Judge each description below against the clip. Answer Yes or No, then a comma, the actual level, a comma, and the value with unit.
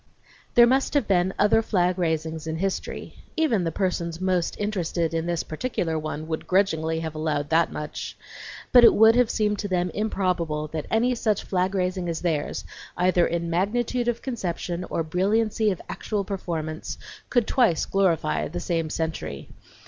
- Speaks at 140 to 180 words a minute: Yes, average, 165 wpm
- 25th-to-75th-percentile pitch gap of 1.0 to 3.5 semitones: No, average, 4.4 semitones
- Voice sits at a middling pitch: Yes, medium, 180 Hz